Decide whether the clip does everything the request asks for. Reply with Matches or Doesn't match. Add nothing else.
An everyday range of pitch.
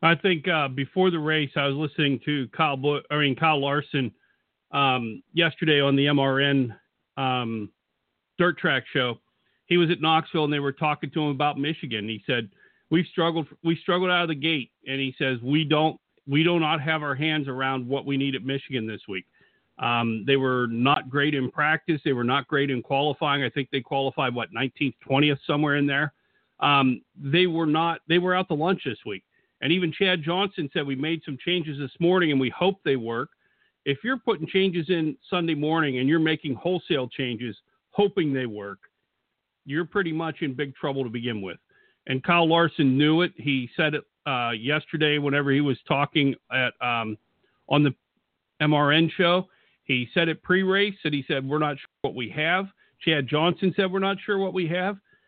Matches